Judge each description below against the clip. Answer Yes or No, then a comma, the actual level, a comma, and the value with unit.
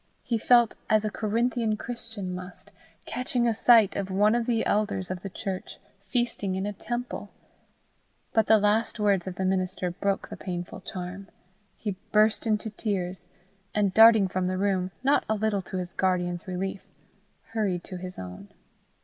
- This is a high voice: Yes, high, 200 Hz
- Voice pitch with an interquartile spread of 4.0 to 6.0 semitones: No, average, 3.0 semitones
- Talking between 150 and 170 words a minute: Yes, average, 165 wpm